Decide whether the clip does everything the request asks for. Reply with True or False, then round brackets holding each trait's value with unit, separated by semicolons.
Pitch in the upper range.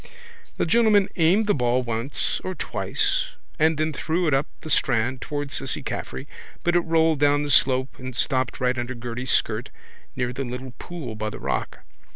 False (135 Hz)